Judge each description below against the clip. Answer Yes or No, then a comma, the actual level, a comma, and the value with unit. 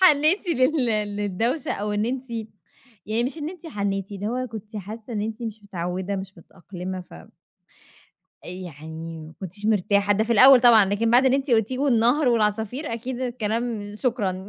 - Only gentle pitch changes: No, average, 4.0 semitones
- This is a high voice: Yes, high, 220 Hz